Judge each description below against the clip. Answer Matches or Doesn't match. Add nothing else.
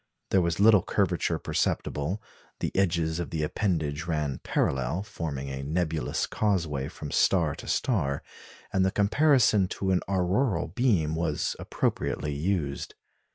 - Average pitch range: Matches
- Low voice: Matches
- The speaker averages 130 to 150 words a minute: Matches